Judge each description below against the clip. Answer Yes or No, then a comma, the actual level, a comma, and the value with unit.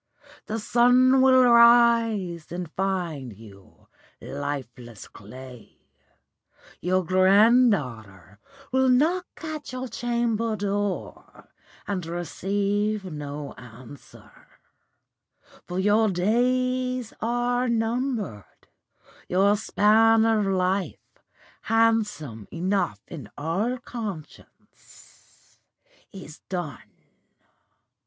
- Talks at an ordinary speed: No, slow, 80 wpm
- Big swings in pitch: Yes, wide, 7.0 semitones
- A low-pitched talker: No, high, 200 Hz